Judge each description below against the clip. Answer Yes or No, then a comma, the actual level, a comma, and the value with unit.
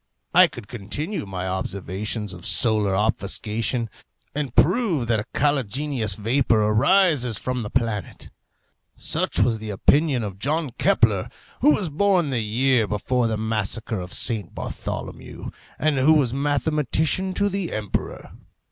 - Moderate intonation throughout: No, wide, 5.8 semitones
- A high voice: No, low, 120 Hz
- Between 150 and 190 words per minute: No, average, 140 wpm